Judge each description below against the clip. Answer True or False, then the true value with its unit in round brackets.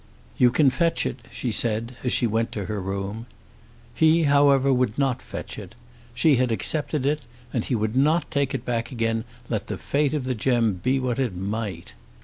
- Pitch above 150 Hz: False (125 Hz)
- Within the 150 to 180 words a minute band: False (195 wpm)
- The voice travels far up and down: False (3.6 semitones)